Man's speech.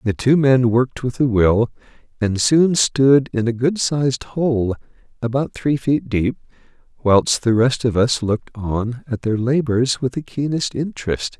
Yes: male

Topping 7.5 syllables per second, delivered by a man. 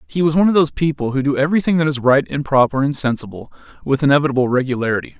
Yes: 7.7 syllables/s; male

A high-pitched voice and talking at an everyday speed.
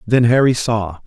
No: low, 115 Hz; average, 170 wpm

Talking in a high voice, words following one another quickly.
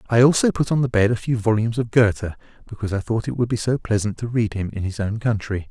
No: low, 110 Hz; fast, 275 wpm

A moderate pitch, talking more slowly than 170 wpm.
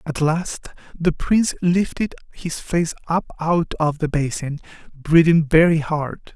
Yes: medium, 160 Hz; average, 140 wpm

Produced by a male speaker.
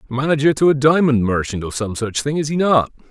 Yes: male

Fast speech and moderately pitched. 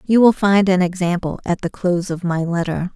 Yes: fast, 225 wpm; medium, 180 Hz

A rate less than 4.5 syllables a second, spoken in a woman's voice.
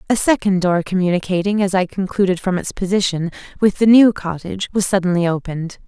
No: 6.0 syllables/s; female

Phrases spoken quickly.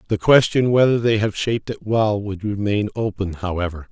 No: average, 185 wpm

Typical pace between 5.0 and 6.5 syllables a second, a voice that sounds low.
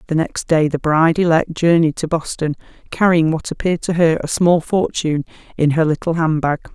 No: 5.6 syllables/s; medium, 160 Hz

